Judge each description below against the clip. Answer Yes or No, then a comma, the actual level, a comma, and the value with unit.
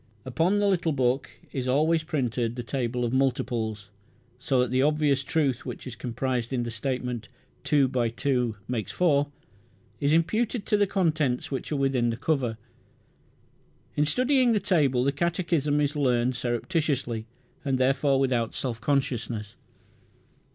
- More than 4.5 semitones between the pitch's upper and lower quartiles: No, average, 3.9 semitones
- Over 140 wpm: Yes, average, 150 wpm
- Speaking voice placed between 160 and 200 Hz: No, low, 135 Hz